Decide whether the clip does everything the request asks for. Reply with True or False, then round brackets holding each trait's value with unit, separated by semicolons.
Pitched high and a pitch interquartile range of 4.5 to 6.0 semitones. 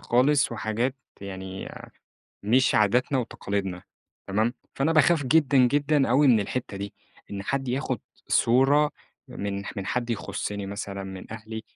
False (115 Hz; 5.0 semitones)